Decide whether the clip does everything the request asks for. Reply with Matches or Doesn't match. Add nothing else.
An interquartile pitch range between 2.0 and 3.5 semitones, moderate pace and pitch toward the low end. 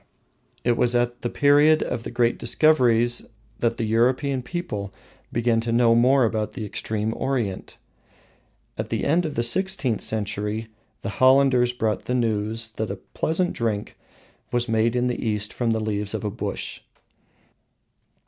Matches